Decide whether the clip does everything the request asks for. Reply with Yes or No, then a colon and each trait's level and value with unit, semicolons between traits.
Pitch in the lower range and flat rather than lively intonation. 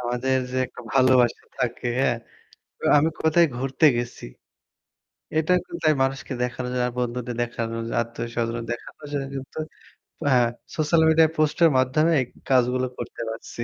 No: low, 130 Hz; average, 3.5 semitones